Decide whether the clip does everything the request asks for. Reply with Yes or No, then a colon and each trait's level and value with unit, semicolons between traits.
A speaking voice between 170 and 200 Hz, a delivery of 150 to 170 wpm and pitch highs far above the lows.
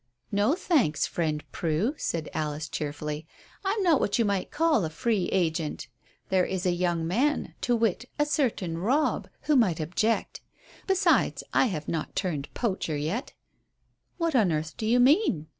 Yes: high, 190 Hz; average, 160 wpm; wide, 8.0 semitones